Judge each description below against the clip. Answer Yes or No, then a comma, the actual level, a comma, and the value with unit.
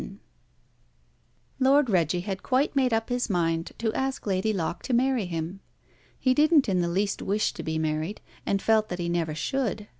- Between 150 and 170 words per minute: No, average, 180 wpm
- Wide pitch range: Yes, wide, 6.6 semitones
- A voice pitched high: Yes, high, 200 Hz